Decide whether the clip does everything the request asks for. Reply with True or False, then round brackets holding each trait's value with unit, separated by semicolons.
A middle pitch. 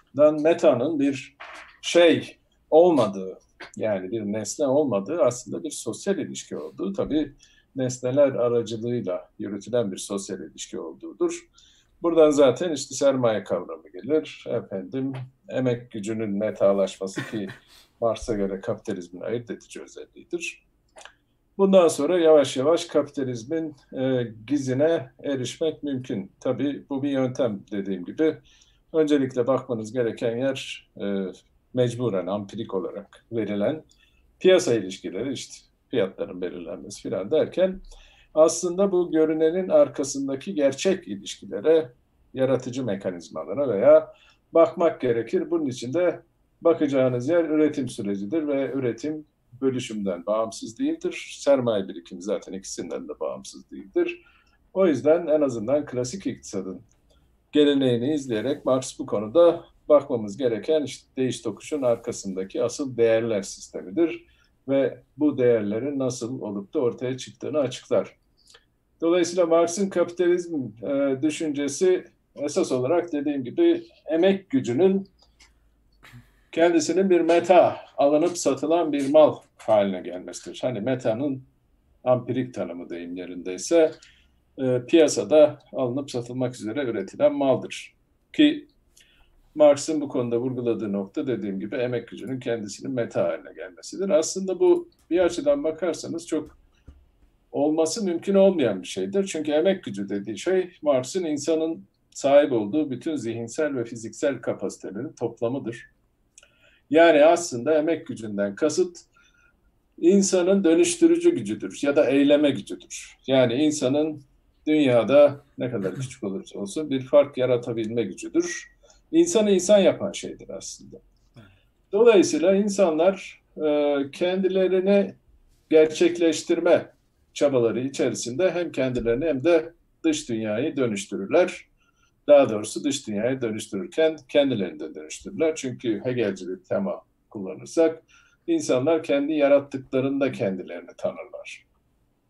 True (145 Hz)